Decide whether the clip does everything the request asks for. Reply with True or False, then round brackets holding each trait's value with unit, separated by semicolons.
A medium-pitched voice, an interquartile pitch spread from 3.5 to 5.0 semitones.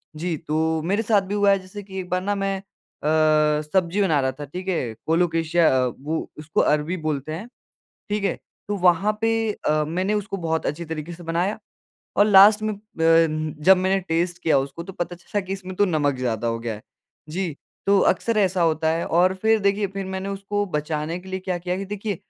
True (175 Hz; 3.9 semitones)